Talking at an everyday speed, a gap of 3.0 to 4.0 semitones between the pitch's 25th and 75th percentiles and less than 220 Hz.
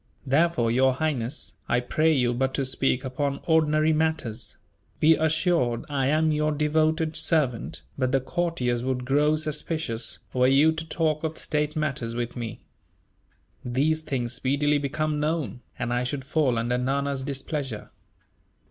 Yes: average, 150 wpm; average, 3.6 semitones; medium, 140 Hz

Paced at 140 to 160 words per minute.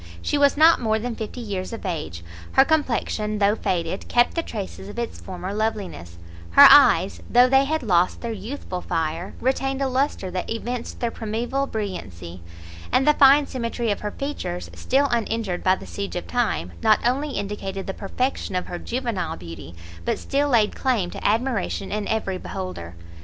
No: average, 180 wpm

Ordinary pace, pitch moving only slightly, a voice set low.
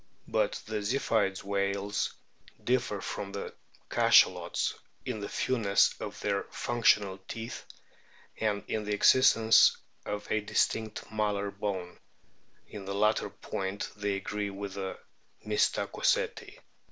No: slow, 115 wpm; narrow, 1.5 semitones; low, 105 Hz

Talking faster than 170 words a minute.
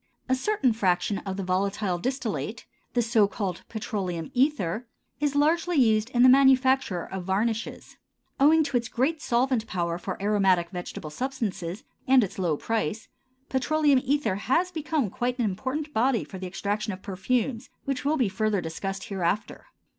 No: average, 160 wpm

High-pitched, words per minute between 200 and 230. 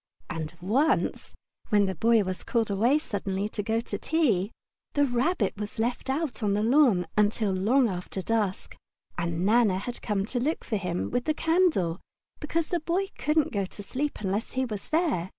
No: high, 220 Hz; average, 190 wpm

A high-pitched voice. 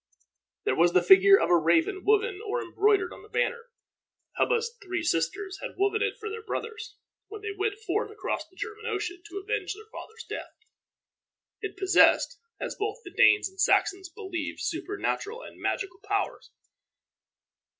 Yes: very high, 405 Hz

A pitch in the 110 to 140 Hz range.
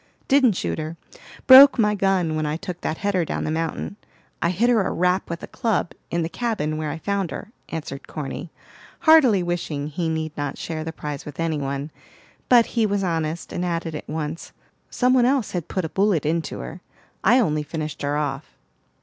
No: medium, 165 Hz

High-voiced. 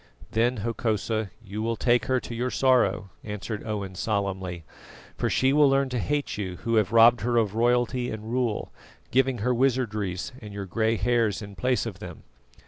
No: low, 115 Hz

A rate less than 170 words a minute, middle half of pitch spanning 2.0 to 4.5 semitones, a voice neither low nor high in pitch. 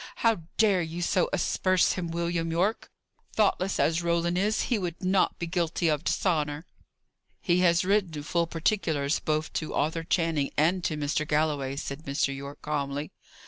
Yes: average, 160 wpm; average, 3.1 semitones; medium, 165 Hz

